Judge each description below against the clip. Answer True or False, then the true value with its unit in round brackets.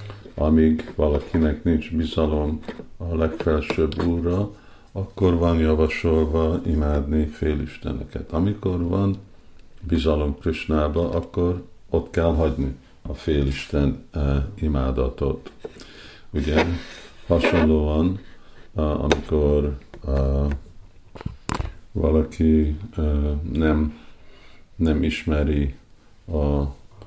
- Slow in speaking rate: True (80 wpm)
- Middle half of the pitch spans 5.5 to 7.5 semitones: False (2.6 semitones)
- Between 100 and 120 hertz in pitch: False (80 Hz)